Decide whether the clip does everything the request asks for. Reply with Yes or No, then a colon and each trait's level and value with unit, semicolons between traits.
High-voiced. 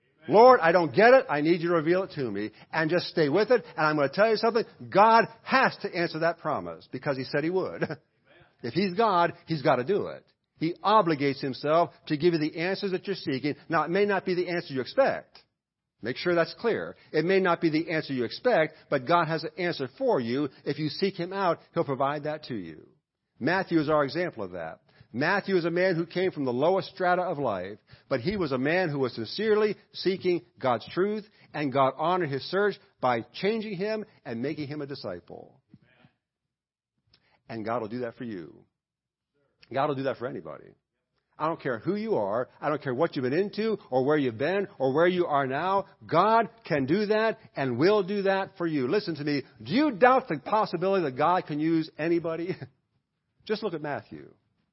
No: medium, 165 Hz